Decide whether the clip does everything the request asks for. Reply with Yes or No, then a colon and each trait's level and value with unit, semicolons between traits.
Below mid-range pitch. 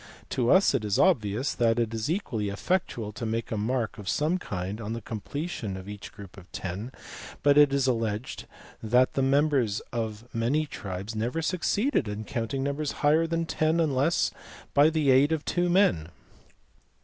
Yes: low, 125 Hz